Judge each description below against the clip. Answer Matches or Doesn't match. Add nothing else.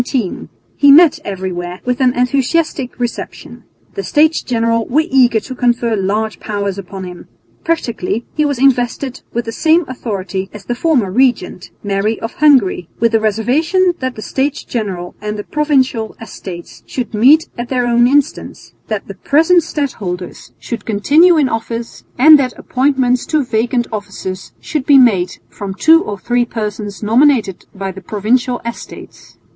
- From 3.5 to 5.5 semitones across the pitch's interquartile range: Matches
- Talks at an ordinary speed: Matches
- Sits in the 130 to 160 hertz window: Doesn't match